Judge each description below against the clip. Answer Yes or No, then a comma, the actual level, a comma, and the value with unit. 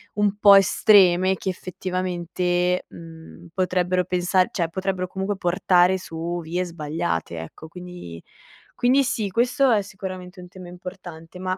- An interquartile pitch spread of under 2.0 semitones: Yes, narrow, 1.6 semitones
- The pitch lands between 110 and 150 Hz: No, medium, 180 Hz